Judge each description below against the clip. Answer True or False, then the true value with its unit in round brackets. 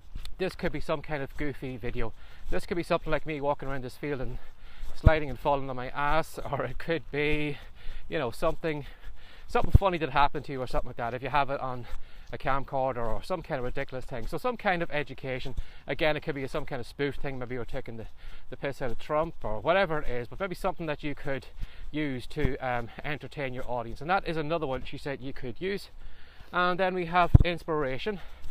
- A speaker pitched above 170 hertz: False (140 Hz)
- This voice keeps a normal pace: False (230 wpm)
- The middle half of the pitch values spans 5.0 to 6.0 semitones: False (4.2 semitones)